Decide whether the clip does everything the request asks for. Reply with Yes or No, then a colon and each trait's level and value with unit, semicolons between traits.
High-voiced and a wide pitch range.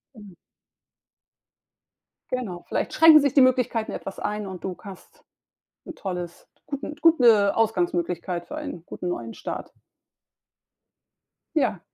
Yes: high, 210 Hz; wide, 6.4 semitones